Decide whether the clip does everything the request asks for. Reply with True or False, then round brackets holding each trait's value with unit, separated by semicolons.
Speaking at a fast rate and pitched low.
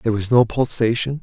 False (195 wpm; 120 Hz)